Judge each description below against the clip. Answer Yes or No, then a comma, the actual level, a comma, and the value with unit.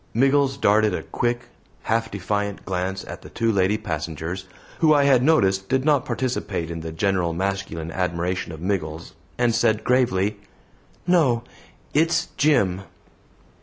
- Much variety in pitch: Yes, wide, 5.7 semitones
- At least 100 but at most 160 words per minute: Yes, average, 140 wpm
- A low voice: Yes, low, 100 Hz